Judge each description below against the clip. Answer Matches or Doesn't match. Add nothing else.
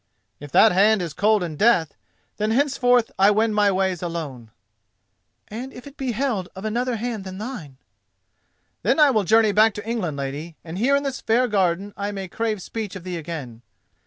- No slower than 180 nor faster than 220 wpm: Matches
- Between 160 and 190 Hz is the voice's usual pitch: Doesn't match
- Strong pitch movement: Doesn't match